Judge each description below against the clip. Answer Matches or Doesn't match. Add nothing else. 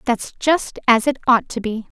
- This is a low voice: Doesn't match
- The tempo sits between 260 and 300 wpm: Doesn't match